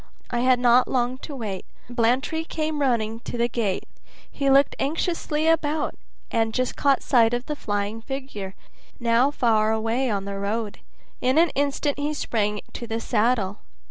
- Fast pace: No, average, 165 wpm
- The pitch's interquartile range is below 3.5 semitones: No, average, 3.9 semitones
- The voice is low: No, high, 245 Hz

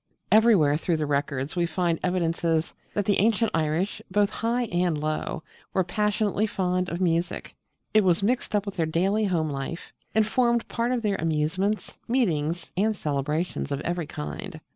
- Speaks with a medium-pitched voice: Yes, medium, 180 Hz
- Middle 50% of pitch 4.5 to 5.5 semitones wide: Yes, average, 4.8 semitones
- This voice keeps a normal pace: Yes, average, 165 wpm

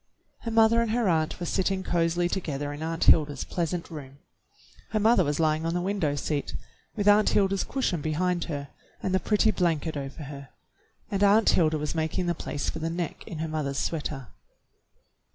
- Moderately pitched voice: Yes, medium, 165 Hz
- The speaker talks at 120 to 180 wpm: No, average, 190 wpm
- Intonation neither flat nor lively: Yes, average, 4.1 semitones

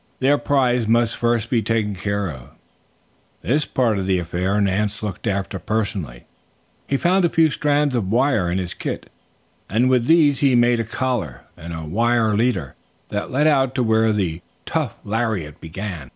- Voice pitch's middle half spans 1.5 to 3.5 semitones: No, average, 4.9 semitones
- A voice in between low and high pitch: No, low, 110 Hz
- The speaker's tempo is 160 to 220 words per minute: Yes, average, 175 wpm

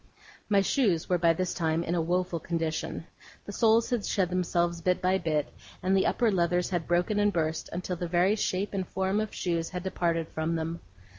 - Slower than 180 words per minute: No, fast, 205 wpm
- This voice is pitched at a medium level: Yes, medium, 180 Hz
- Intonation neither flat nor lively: No, narrow, 2.3 semitones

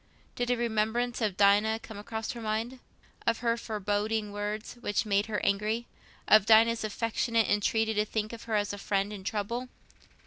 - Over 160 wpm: Yes, average, 180 wpm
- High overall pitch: Yes, high, 220 Hz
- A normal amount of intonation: No, narrow, 1.9 semitones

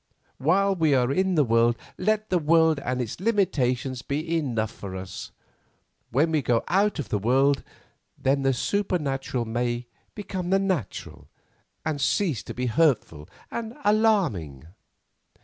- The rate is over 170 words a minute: No, average, 145 wpm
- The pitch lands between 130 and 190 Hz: Yes, medium, 140 Hz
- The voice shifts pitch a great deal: Yes, wide, 7.3 semitones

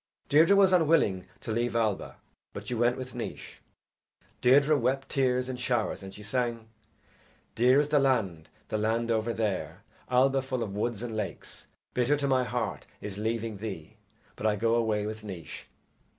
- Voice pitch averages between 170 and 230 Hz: No, low, 115 Hz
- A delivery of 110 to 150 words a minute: No, average, 170 wpm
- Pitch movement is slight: No, average, 3.4 semitones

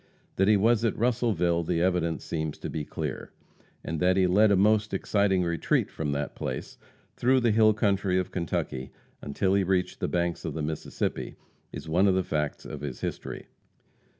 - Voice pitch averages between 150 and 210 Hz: No, very low, 90 Hz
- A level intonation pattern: No, average, 4.0 semitones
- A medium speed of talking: Yes, average, 185 wpm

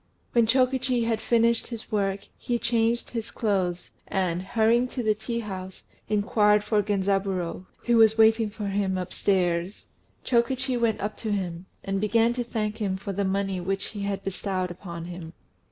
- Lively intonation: No, average, 3.3 semitones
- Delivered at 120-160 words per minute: No, average, 170 wpm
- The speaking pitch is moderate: No, high, 210 Hz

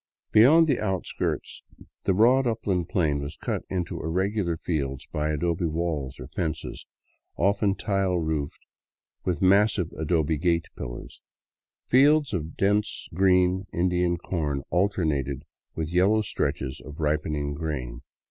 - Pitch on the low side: Yes, very low, 85 Hz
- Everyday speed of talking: No, slow, 130 wpm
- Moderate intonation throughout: Yes, average, 4.3 semitones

